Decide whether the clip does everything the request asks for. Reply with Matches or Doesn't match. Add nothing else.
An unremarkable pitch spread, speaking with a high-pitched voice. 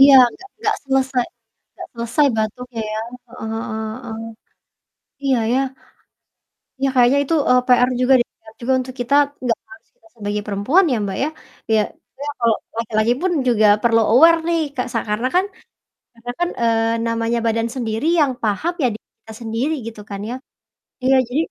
Matches